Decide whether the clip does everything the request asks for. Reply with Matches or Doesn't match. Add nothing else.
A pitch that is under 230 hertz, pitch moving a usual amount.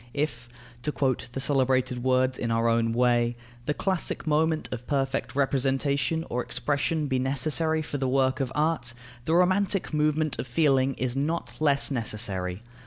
Matches